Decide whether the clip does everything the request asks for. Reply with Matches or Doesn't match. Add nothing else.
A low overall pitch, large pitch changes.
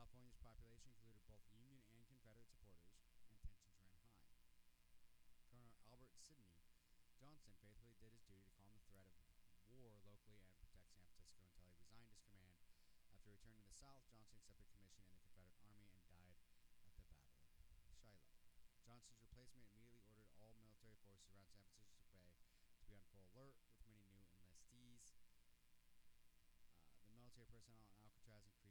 Doesn't match